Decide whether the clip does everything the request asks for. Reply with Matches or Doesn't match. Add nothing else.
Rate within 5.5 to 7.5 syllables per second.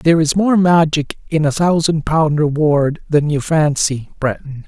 Doesn't match